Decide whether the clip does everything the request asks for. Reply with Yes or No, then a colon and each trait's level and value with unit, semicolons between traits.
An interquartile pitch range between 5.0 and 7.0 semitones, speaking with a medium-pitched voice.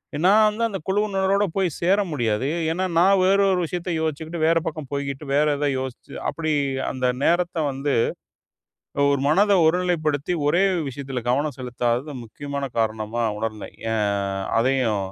Yes: wide, 5.6 semitones; medium, 150 Hz